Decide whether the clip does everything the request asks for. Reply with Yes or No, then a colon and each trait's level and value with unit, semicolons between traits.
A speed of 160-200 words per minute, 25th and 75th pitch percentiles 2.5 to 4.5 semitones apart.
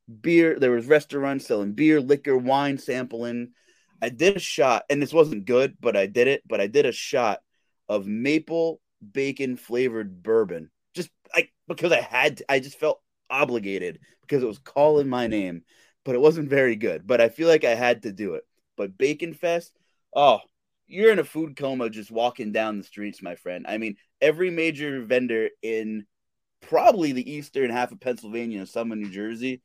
No: average, 190 wpm; wide, 5.5 semitones